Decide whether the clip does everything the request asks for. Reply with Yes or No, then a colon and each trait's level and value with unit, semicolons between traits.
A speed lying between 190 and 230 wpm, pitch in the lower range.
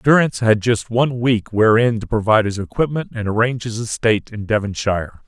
No: average, 180 wpm; low, 110 Hz